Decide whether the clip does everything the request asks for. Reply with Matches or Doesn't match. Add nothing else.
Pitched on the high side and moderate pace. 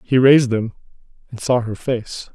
Doesn't match